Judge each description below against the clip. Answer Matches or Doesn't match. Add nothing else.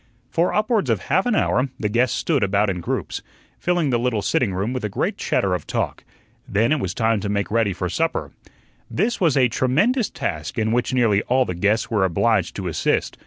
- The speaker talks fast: Matches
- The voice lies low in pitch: Matches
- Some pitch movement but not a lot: Doesn't match